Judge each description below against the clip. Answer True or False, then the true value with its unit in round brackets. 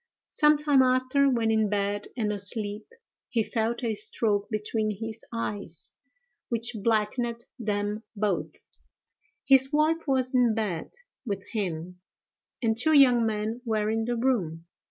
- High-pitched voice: True (225 Hz)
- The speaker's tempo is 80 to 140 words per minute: True (135 wpm)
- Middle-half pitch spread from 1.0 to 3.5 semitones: True (3.1 semitones)